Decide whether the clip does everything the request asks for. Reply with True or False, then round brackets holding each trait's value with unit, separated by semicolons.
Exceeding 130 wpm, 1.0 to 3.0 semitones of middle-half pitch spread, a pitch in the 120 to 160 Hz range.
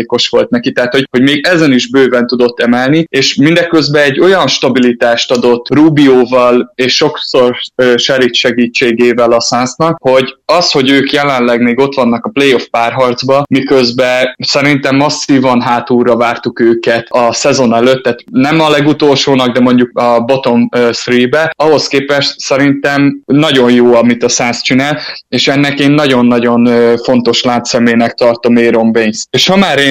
True (155 wpm; 2.7 semitones; 125 Hz)